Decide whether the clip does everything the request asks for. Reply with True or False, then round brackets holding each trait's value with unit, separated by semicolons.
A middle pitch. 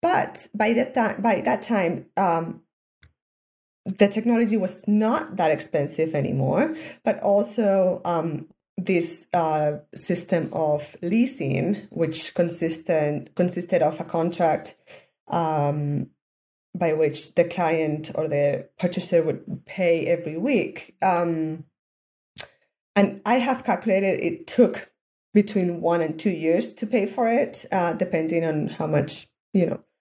True (170 Hz)